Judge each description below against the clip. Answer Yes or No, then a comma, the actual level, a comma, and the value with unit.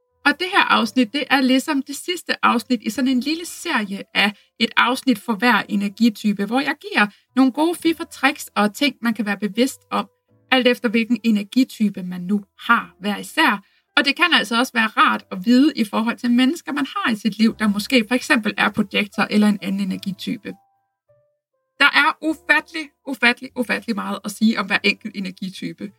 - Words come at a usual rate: Yes, average, 195 wpm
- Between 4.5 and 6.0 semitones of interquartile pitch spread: Yes, average, 4.9 semitones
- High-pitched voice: Yes, high, 245 Hz